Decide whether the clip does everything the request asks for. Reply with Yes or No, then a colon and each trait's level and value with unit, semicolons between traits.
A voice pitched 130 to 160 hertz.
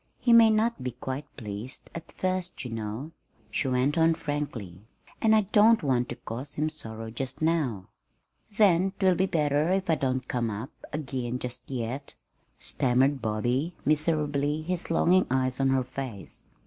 Yes: medium, 140 Hz